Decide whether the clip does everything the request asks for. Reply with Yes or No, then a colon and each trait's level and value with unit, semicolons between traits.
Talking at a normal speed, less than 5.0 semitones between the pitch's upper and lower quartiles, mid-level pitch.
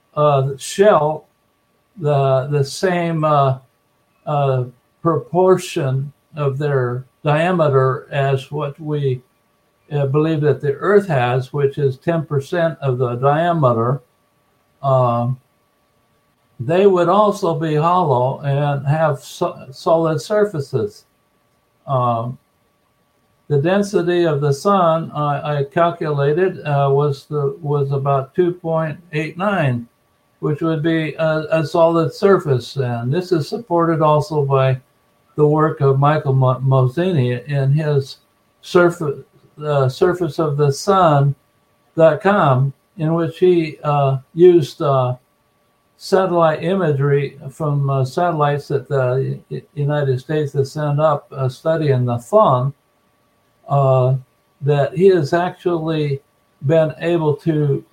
No: slow, 115 wpm; average, 3.3 semitones; medium, 145 Hz